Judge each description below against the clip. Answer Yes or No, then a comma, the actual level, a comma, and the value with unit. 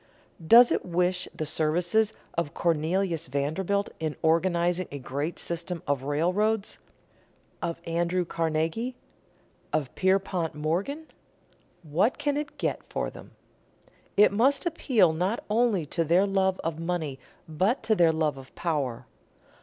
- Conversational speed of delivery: No, slow, 130 wpm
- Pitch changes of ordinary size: Yes, average, 4.0 semitones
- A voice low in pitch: No, medium, 170 Hz